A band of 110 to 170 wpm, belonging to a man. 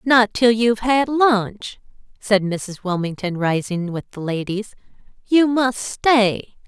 No: slow, 135 wpm; female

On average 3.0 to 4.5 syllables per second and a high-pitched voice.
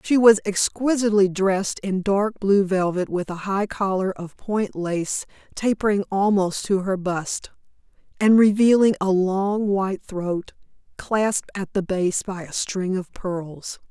Yes: 4.0 syllables/s; high, 195 Hz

